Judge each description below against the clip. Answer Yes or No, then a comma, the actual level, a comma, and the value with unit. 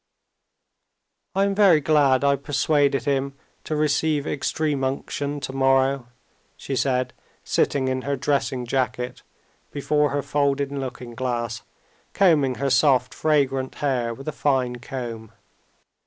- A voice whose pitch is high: No, low, 135 Hz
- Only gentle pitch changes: Yes, narrow, 1.9 semitones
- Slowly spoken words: Yes, slow, 125 wpm